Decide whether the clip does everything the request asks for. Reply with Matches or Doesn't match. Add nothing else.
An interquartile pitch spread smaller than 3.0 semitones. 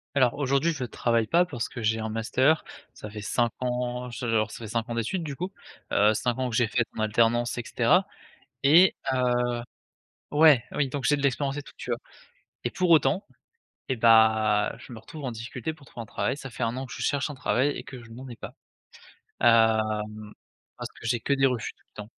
Doesn't match